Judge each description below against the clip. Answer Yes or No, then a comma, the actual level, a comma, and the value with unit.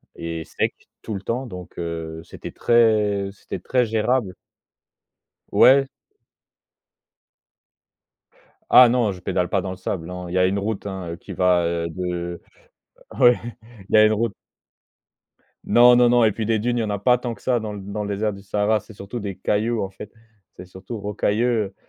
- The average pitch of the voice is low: Yes, low, 105 Hz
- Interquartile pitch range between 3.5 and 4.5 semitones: Yes, average, 4.0 semitones